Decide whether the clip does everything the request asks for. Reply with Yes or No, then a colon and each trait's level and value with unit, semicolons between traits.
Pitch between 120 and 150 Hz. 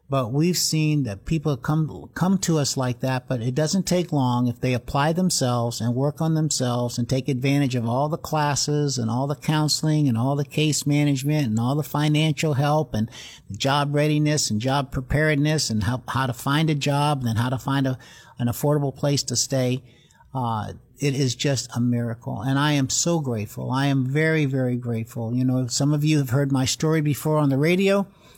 Yes: medium, 140 Hz